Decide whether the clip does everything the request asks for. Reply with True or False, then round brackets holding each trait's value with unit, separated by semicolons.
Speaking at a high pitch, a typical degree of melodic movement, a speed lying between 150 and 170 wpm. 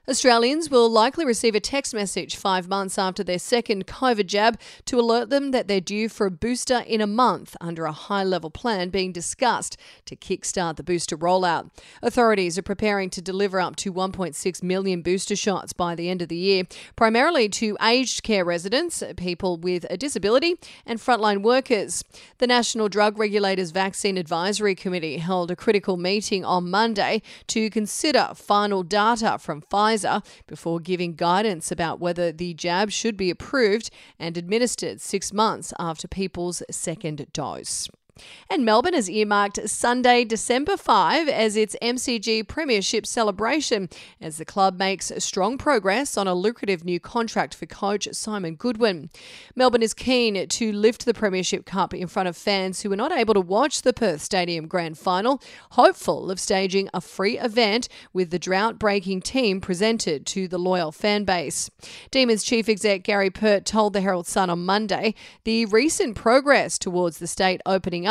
True (200 Hz; 3.7 semitones; 165 wpm)